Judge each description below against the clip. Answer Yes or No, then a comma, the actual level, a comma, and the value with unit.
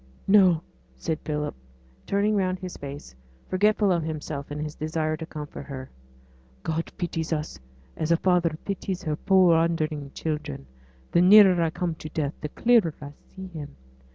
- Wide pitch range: No, average, 3.4 semitones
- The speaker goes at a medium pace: Yes, average, 160 wpm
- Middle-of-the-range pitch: Yes, medium, 165 Hz